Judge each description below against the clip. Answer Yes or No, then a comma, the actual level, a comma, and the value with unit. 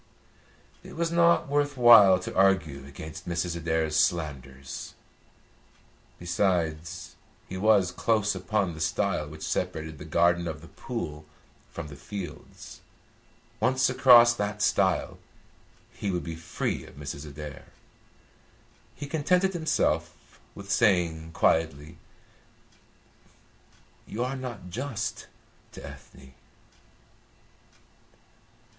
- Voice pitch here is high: No, very low, 90 Hz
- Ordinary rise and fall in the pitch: No, wide, 6.5 semitones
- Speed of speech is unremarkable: No, slow, 105 wpm